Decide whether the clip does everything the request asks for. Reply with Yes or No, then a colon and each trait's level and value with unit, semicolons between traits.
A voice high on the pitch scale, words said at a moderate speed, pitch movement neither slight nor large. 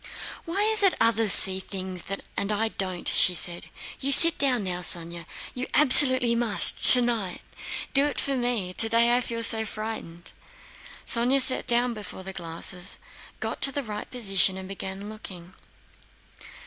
Yes: high, 220 Hz; average, 150 wpm; average, 4.8 semitones